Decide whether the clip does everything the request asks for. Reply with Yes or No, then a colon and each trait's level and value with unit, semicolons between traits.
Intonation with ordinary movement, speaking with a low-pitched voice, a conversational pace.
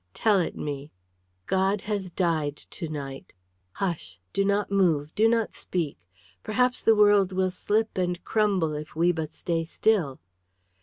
No: average, 4.6 semitones; medium, 185 Hz; average, 150 wpm